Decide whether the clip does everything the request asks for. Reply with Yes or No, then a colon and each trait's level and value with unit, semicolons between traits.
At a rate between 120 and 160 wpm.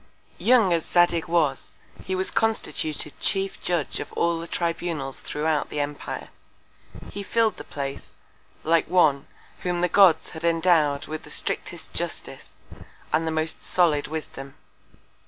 Yes: average, 140 wpm